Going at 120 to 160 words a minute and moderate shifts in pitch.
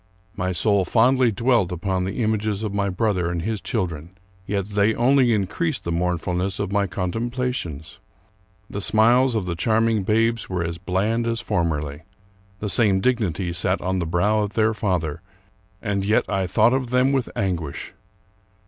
No: average, 170 wpm; average, 4.0 semitones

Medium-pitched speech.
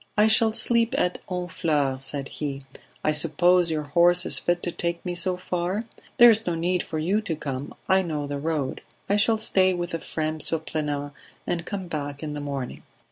Yes: medium, 170 Hz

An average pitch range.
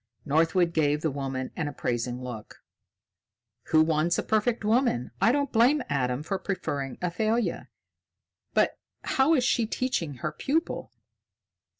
No: wide, 8.6 semitones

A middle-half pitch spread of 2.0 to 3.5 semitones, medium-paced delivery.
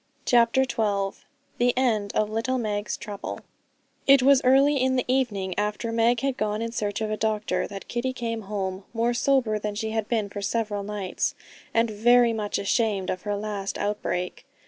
Yes: average, 2.8 semitones; average, 180 wpm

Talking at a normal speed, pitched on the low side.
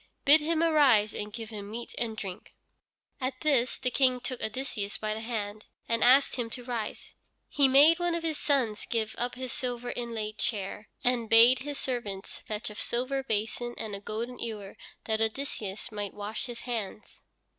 No: average, 180 wpm; high, 235 Hz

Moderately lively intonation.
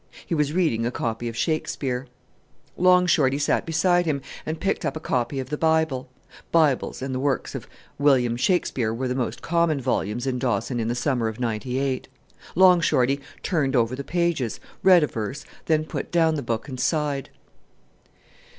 Yes: average, 4.5 semitones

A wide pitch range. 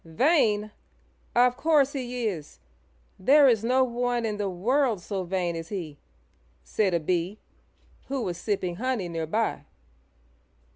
Yes: wide, 5.8 semitones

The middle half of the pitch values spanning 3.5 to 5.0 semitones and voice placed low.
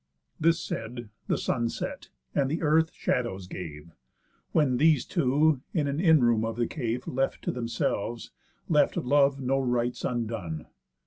Yes: average, 4.0 semitones; low, 125 Hz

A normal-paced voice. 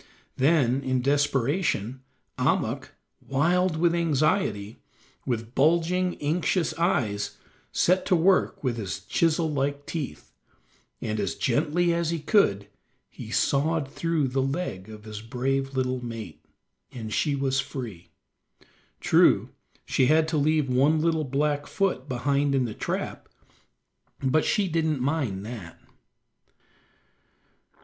No: slow, 125 wpm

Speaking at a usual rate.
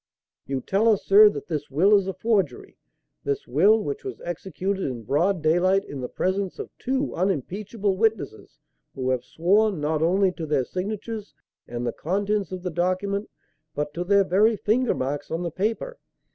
Yes: average, 175 wpm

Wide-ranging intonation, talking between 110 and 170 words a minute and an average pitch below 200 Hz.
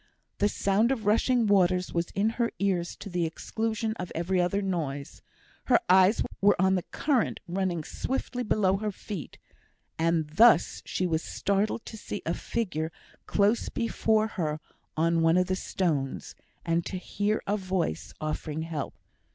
No: average, 4.2 semitones; average, 160 wpm; high, 190 Hz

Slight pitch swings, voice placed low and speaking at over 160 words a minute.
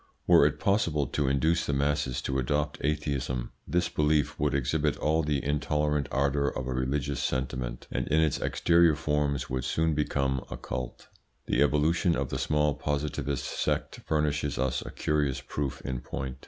Yes: narrow, 2.1 semitones; very low, 75 Hz; average, 170 wpm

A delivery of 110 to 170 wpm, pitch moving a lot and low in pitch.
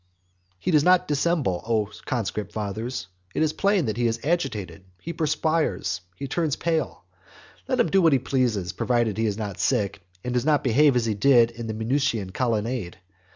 No: average, 190 wpm; wide, 5.8 semitones; low, 120 Hz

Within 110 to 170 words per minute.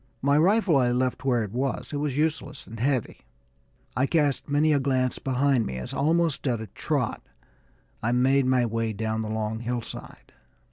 No: average, 180 wpm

